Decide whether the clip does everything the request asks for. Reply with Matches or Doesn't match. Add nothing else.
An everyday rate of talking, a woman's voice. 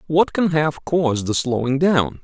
Doesn't match